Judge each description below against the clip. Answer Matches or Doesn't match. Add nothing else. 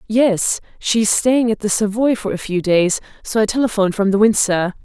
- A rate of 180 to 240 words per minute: Matches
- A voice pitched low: Doesn't match